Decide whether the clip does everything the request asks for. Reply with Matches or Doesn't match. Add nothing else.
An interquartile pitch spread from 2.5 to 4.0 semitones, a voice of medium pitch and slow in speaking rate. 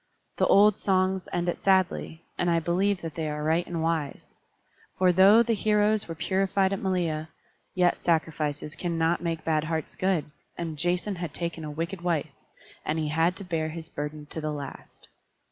Doesn't match